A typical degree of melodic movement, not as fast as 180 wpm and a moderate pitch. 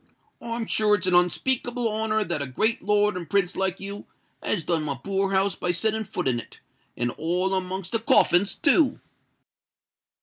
No: average, 3.6 semitones; average, 170 wpm; high, 195 Hz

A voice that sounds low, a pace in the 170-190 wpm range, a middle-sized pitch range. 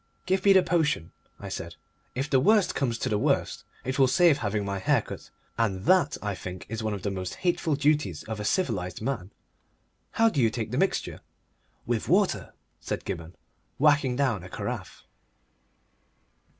No: low, 125 Hz; average, 175 wpm; wide, 7.0 semitones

